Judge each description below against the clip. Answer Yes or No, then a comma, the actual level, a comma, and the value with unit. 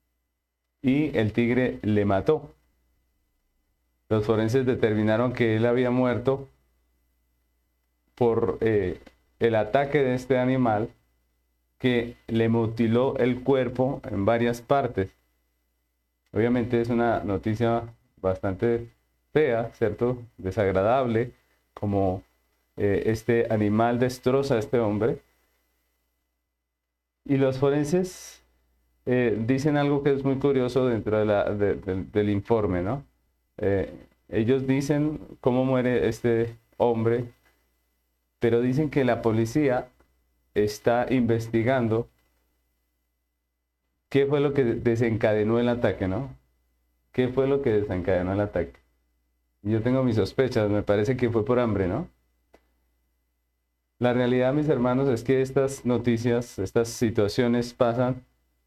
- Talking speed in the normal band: No, slow, 115 wpm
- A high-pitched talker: No, low, 110 Hz